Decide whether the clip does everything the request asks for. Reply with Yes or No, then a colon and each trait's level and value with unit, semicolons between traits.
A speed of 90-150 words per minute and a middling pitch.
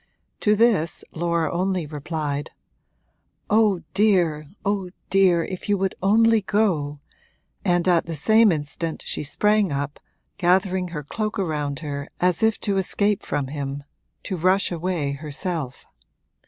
Yes: slow, 135 wpm; medium, 175 Hz